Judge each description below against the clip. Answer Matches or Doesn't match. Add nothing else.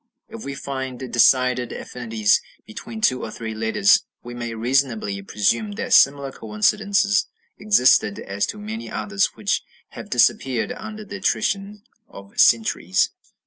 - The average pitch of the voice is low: Matches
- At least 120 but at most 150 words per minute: Matches